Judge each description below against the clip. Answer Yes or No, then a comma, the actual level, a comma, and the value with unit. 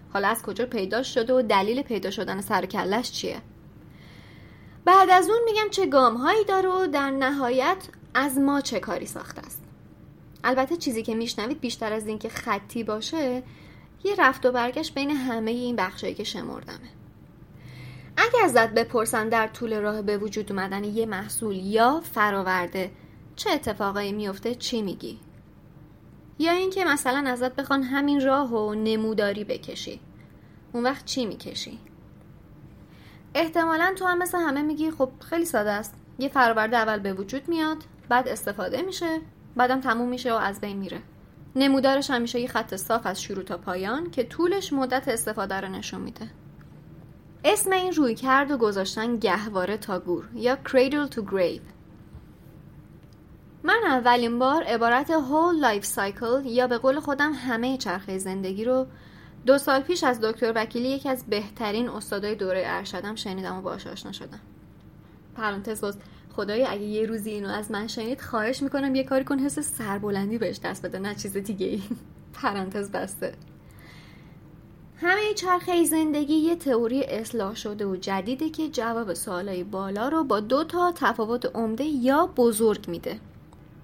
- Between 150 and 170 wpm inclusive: Yes, fast, 155 wpm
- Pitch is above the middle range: Yes, high, 240 Hz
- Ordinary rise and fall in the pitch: Yes, average, 5.0 semitones